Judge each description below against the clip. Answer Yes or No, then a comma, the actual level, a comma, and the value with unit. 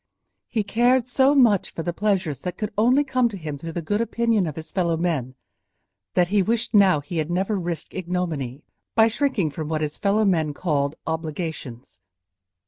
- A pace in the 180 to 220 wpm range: Yes, average, 185 wpm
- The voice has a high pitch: No, medium, 180 Hz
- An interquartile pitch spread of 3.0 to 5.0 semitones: No, wide, 5.5 semitones